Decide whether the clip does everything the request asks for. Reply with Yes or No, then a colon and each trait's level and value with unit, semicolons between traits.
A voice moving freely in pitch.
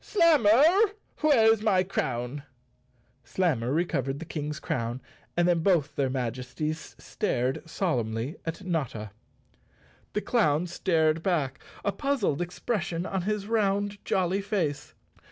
Yes: wide, 7.0 semitones